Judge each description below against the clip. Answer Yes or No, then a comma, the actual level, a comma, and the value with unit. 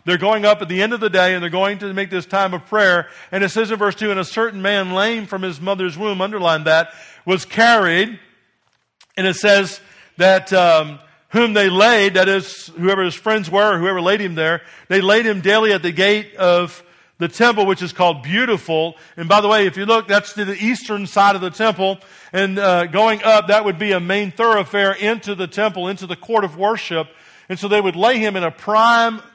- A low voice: No, high, 195 Hz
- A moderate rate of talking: No, fast, 230 wpm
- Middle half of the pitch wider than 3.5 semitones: No, narrow, 2.5 semitones